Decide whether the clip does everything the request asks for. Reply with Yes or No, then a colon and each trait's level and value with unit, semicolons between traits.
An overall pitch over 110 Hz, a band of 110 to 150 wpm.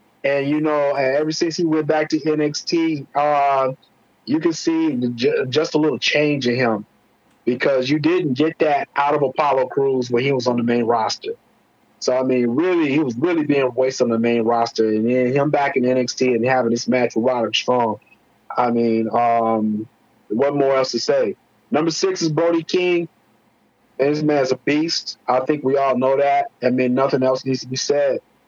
No: medium, 140 Hz; average, 200 wpm